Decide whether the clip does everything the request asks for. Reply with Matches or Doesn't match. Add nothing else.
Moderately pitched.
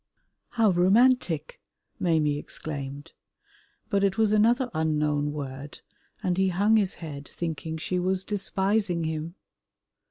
Matches